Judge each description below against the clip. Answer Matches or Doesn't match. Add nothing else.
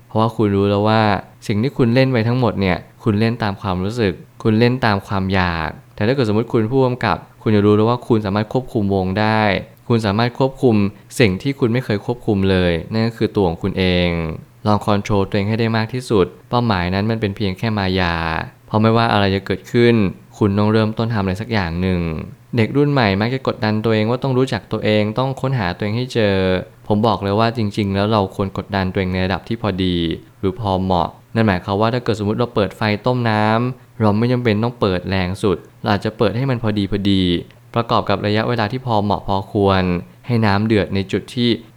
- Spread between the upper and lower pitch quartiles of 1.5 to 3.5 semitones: Matches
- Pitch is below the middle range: Matches